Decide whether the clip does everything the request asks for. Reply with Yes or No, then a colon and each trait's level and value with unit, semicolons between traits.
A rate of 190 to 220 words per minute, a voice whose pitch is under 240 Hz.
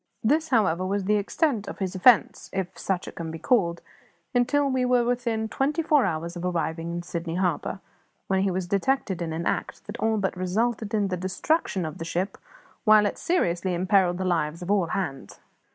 Yes: average, 200 wpm; high, 190 Hz